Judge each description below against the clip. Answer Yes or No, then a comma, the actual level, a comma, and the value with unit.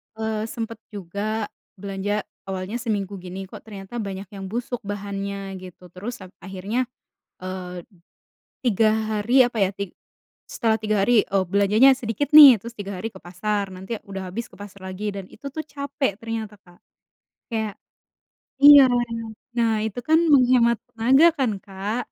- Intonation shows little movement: No, average, 3.3 semitones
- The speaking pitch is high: Yes, high, 210 Hz